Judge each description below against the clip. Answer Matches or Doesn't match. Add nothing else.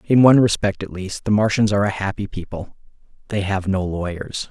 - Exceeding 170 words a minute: Matches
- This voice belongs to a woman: Doesn't match